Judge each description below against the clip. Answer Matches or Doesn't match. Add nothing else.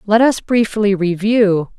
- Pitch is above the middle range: Matches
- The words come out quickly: Doesn't match